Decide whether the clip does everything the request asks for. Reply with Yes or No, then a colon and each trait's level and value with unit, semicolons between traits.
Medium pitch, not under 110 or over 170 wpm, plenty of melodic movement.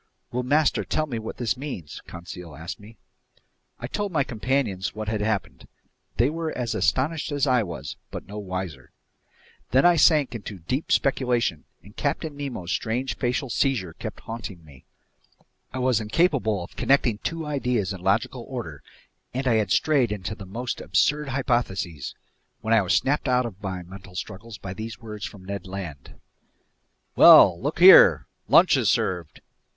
No: low, 115 Hz; average, 165 wpm; wide, 5.9 semitones